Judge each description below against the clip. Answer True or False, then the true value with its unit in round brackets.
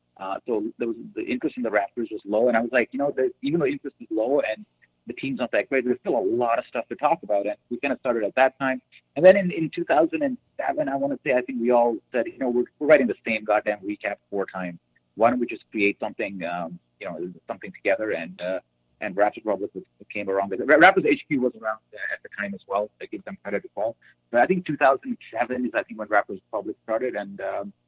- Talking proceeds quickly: True (270 wpm)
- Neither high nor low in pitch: False (115 Hz)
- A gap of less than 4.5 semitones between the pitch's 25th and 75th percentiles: False (4.9 semitones)